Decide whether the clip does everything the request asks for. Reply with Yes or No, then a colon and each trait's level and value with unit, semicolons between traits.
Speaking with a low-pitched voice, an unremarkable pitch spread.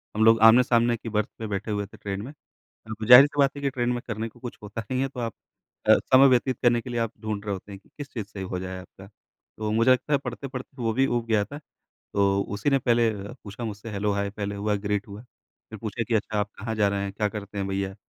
Yes: low, 110 Hz; average, 3.1 semitones